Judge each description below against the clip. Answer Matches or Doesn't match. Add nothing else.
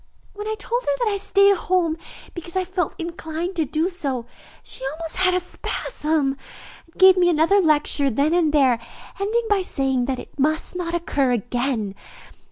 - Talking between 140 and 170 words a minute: Doesn't match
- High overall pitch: Matches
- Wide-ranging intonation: Doesn't match